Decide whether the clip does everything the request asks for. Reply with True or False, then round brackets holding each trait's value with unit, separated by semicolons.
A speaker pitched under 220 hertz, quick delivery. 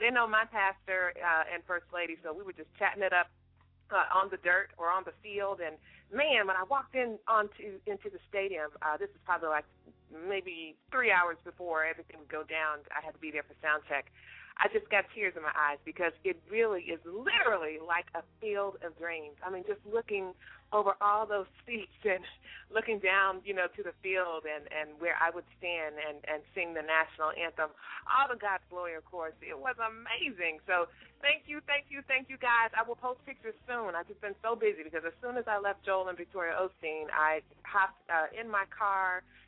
True (185 Hz; 215 wpm)